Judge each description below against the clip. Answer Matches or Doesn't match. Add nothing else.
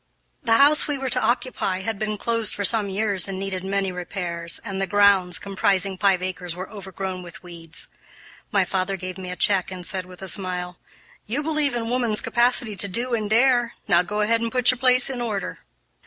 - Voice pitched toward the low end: Doesn't match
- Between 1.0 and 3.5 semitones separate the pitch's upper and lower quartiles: Doesn't match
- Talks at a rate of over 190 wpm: Matches